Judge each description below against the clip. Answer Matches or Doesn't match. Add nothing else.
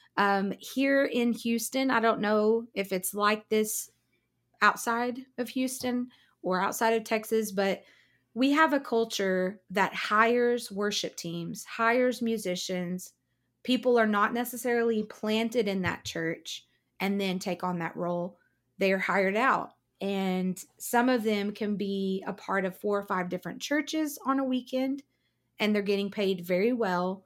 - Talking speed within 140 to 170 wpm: Matches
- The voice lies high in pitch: Matches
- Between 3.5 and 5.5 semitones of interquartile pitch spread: Matches